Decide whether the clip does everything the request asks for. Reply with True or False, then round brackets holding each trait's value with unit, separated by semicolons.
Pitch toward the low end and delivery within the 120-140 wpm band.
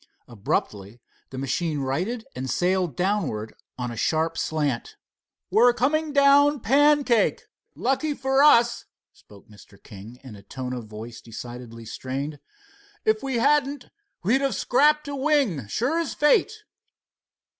False (185 Hz; 135 wpm)